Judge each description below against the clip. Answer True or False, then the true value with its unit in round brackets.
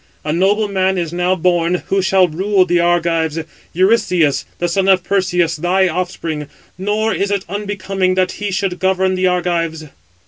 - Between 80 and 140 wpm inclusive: False (165 wpm)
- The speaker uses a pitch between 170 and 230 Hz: True (185 Hz)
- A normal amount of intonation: False (1.9 semitones)